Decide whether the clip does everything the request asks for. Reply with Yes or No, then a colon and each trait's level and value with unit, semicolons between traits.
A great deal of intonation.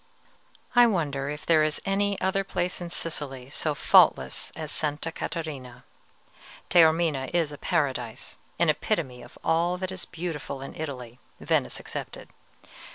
No: average, 4.1 semitones